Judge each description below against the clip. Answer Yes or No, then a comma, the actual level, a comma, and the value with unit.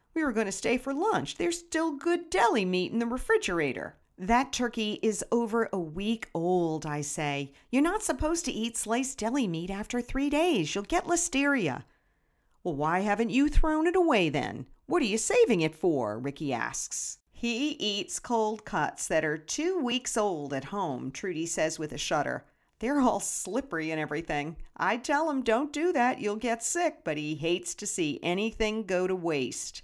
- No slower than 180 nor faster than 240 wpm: Yes, average, 185 wpm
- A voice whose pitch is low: No, high, 225 Hz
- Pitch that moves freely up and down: Yes, wide, 8.5 semitones